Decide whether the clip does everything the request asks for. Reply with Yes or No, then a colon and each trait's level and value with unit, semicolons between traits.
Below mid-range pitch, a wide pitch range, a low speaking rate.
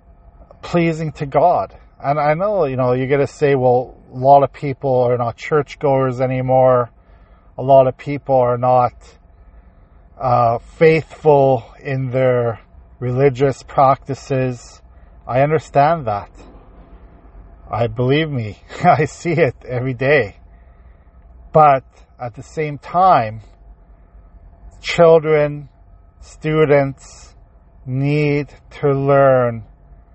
Yes: low, 125 Hz; wide, 8.4 semitones; slow, 105 wpm